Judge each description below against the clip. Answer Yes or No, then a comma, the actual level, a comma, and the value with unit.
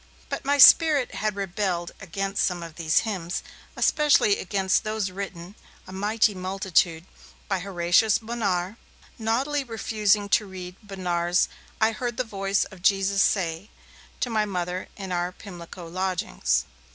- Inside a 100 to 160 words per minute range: Yes, average, 140 wpm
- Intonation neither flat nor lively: Yes, average, 3.3 semitones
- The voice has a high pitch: Yes, high, 195 Hz